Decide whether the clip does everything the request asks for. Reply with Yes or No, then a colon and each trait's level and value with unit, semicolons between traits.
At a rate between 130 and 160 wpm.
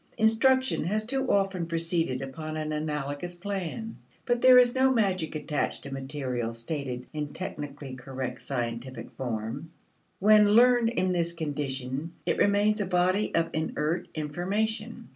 Yes: average, 140 wpm